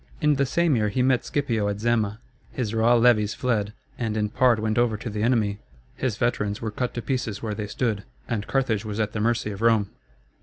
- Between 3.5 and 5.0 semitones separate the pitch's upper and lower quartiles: No, narrow, 2.6 semitones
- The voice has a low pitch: Yes, low, 110 Hz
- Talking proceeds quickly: Yes, fast, 220 wpm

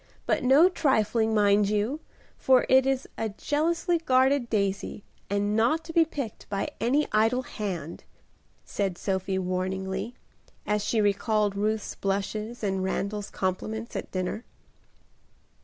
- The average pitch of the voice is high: Yes, high, 215 Hz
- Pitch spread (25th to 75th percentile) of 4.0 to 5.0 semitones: Yes, average, 4.4 semitones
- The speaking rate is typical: No, slow, 130 wpm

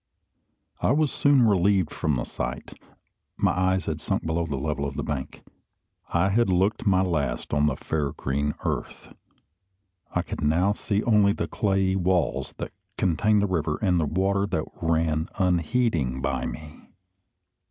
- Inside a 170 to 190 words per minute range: No, average, 160 wpm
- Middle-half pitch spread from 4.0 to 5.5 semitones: Yes, average, 4.8 semitones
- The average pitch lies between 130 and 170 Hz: No, very low, 90 Hz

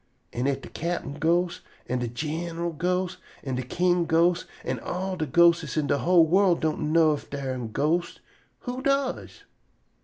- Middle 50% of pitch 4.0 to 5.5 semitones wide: No, average, 3.6 semitones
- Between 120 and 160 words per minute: No, average, 175 wpm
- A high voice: No, medium, 165 Hz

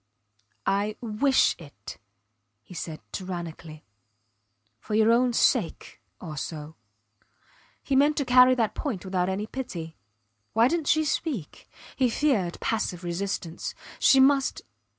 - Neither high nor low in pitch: No, high, 210 Hz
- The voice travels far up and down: Yes, wide, 7.1 semitones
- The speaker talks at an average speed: No, slow, 120 wpm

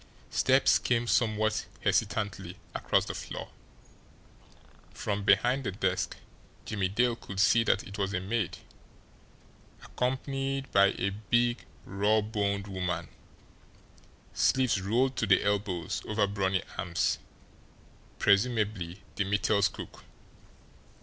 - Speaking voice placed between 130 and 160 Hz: No, low, 105 Hz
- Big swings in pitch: No, average, 3.2 semitones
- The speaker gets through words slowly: Yes, slow, 110 wpm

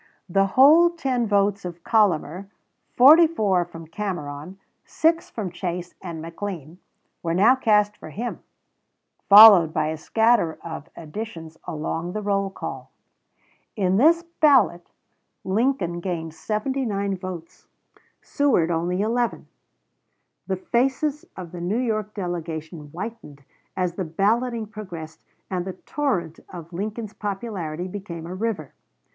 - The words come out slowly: Yes, slow, 125 wpm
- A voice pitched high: Yes, high, 195 Hz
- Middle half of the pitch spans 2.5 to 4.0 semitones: No, average, 4.8 semitones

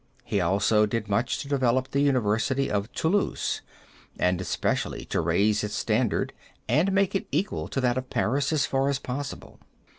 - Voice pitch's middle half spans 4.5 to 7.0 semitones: Yes, average, 5.0 semitones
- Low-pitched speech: Yes, low, 125 Hz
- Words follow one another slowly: No, average, 170 wpm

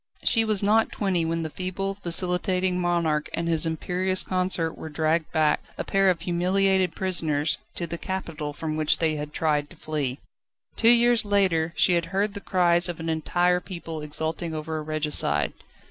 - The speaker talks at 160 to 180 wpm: Yes, average, 175 wpm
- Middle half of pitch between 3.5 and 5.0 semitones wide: No, average, 2.9 semitones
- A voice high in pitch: No, medium, 170 Hz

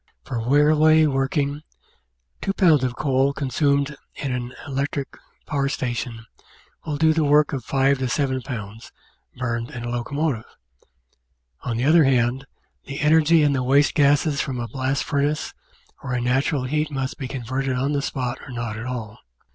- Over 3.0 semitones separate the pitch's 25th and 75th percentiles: No, average, 2.7 semitones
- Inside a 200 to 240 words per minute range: No, average, 165 wpm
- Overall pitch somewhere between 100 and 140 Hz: Yes, low, 135 Hz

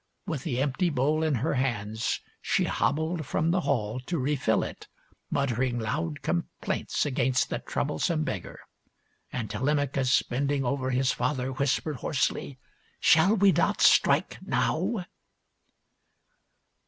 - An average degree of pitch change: Yes, average, 3.6 semitones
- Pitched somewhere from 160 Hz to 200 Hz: No, low, 135 Hz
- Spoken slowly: Yes, slow, 130 wpm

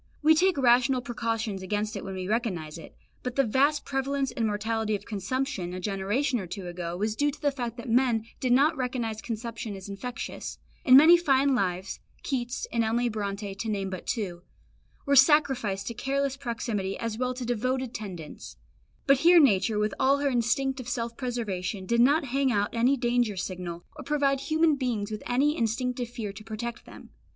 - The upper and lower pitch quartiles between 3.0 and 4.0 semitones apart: No, average, 4.4 semitones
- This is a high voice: Yes, high, 235 Hz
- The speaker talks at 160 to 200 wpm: Yes, average, 190 wpm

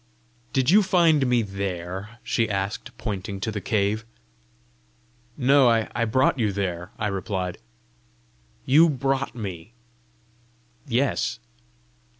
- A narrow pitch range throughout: No, average, 5.0 semitones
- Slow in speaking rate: Yes, slow, 110 wpm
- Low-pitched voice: Yes, low, 110 Hz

